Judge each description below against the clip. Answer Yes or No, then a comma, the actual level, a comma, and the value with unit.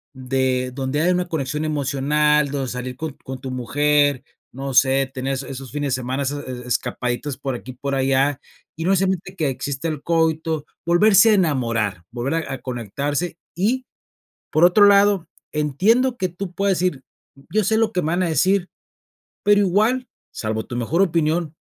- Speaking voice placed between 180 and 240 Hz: No, medium, 145 Hz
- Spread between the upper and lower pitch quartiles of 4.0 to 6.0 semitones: Yes, average, 5.1 semitones